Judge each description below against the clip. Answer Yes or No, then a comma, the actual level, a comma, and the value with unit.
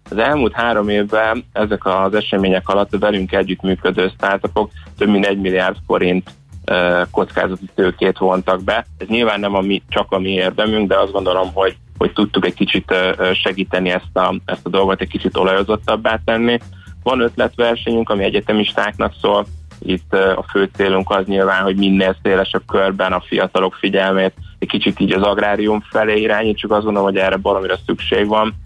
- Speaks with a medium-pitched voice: No, very low, 95 Hz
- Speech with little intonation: Yes, narrow, 1.9 semitones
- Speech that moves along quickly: Yes, fast, 170 wpm